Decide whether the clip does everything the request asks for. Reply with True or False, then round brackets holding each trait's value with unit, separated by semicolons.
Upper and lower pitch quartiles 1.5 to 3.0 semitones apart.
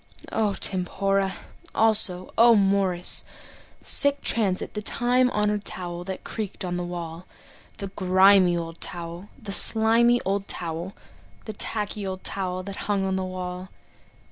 True (2.5 semitones)